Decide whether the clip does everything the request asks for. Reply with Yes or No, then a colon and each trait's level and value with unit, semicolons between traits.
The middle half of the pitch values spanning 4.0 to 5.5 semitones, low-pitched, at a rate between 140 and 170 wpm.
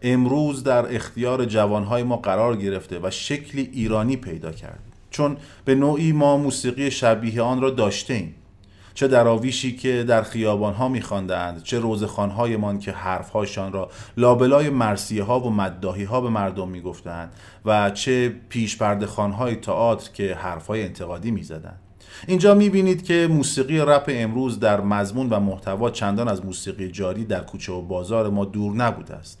Yes: average, 4.3 semitones; low, 110 Hz; average, 150 wpm